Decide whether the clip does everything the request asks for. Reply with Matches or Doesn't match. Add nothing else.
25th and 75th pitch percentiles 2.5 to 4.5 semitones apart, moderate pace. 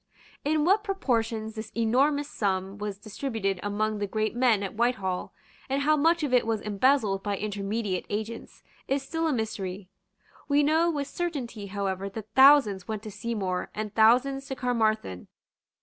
Doesn't match